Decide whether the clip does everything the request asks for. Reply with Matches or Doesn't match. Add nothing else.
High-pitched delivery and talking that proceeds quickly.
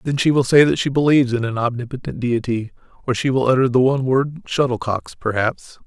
Doesn't match